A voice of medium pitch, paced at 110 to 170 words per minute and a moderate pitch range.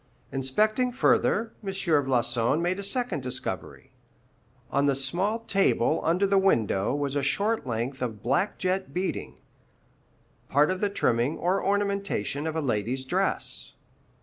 No: medium, 160 Hz; average, 140 wpm; wide, 7.1 semitones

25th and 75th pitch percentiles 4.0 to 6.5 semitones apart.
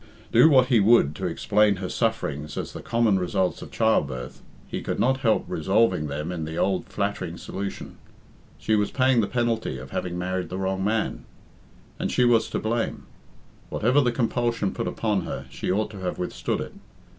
Yes: average, 4.3 semitones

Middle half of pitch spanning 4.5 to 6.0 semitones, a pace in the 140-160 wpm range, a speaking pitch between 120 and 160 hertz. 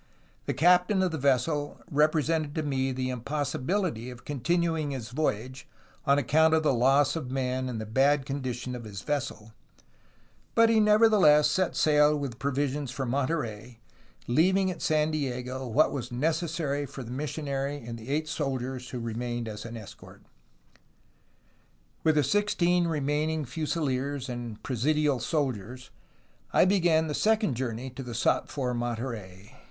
No: average, 3.9 semitones; average, 150 wpm; medium, 140 Hz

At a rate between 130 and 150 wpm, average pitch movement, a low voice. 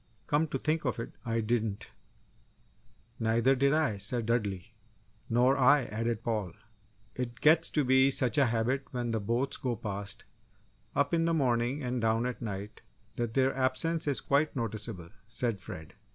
No: average, 165 wpm; average, 3.4 semitones; low, 120 Hz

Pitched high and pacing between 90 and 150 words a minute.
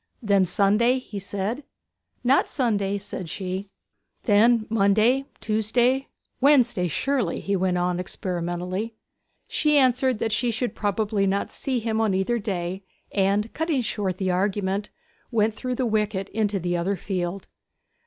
Yes: high, 205 Hz; average, 140 wpm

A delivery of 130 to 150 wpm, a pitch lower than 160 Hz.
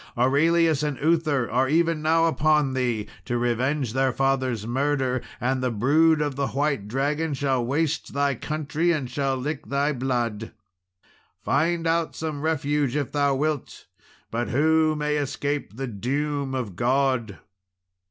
Yes: average, 145 wpm; medium, 140 Hz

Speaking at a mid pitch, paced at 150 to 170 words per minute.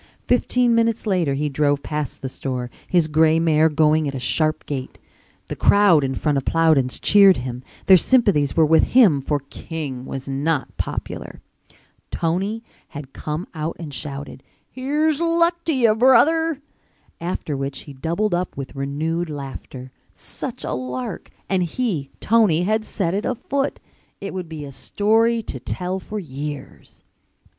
Yes: medium, 160 Hz; average, 155 wpm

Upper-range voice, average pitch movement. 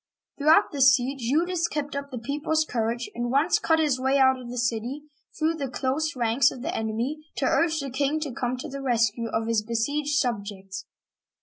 Yes: very high, 260 Hz; average, 3.8 semitones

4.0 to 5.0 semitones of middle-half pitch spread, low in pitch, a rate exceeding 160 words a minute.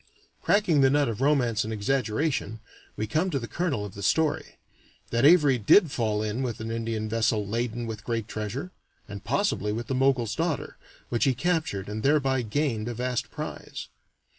Yes: average, 4.5 semitones; low, 120 Hz; average, 180 wpm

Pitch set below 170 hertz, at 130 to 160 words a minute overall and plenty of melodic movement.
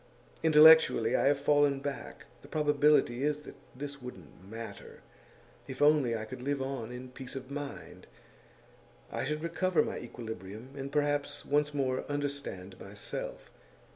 No: medium, 140 Hz; average, 140 wpm; average, 3.0 semitones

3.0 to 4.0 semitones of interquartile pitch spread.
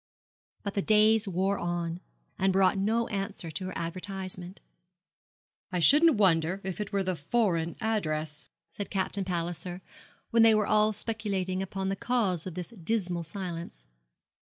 Yes: average, 3.3 semitones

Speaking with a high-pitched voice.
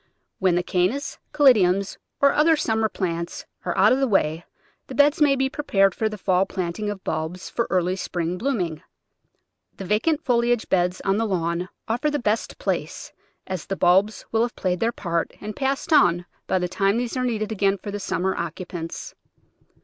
Yes: high, 195 Hz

